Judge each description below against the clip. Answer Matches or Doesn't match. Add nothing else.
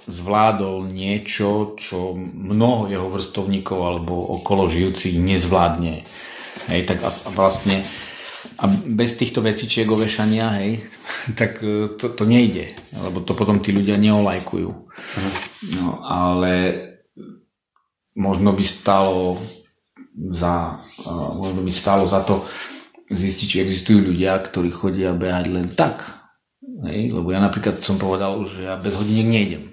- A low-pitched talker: Matches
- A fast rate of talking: Doesn't match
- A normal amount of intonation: Doesn't match